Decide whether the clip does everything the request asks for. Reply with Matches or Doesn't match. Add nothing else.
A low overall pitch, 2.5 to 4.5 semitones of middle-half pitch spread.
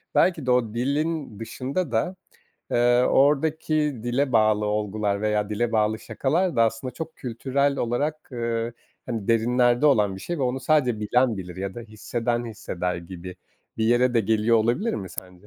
Matches